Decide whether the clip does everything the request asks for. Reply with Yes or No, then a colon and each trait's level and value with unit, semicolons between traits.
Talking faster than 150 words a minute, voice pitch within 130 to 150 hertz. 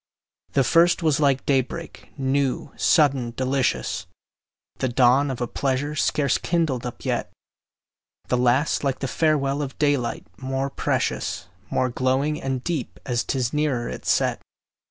No: average, 145 wpm; low, 135 Hz